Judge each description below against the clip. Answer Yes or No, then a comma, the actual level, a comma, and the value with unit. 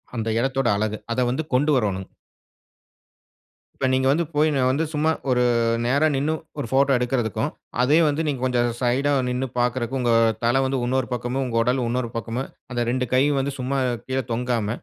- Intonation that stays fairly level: Yes, narrow, 2.0 semitones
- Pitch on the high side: No, low, 130 Hz